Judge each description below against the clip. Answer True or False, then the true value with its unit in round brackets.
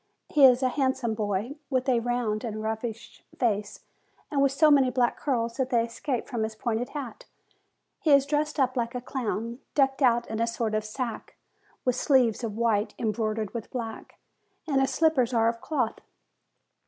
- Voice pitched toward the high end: True (240 Hz)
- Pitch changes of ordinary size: True (3.0 semitones)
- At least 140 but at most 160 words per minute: False (180 wpm)